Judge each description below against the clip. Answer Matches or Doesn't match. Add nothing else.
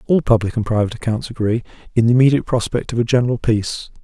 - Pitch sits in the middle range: Doesn't match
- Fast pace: Matches